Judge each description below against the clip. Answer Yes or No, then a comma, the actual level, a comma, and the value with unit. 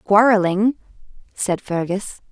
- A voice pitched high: Yes, high, 200 Hz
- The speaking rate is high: No, slow, 80 wpm